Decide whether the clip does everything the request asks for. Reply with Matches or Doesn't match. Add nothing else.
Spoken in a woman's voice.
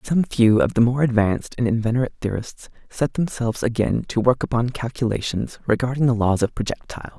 Doesn't match